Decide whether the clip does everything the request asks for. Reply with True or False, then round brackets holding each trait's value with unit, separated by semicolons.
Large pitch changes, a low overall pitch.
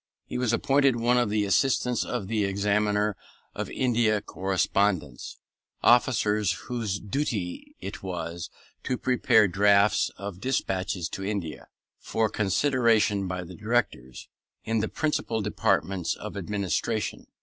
False (3.2 semitones; 105 Hz)